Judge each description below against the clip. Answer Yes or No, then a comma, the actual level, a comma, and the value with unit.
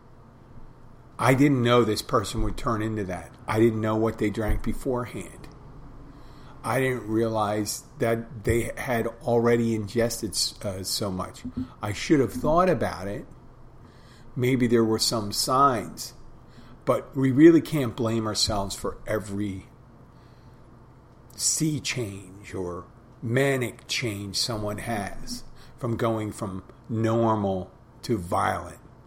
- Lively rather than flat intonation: No, average, 2.8 semitones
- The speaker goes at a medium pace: No, slow, 120 wpm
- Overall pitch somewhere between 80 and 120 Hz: Yes, low, 115 Hz